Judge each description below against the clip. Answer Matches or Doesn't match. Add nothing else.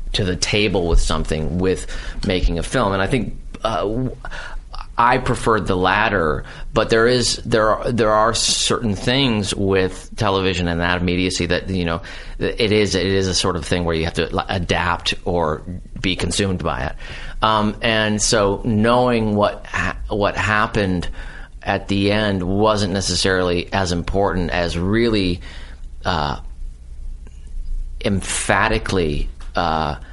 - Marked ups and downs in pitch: Doesn't match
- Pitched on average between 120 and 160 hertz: Doesn't match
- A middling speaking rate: Matches